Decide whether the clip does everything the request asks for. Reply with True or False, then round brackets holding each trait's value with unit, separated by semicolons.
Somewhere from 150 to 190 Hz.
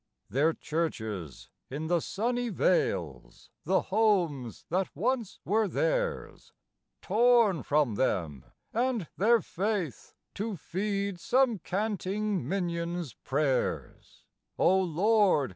True (185 Hz)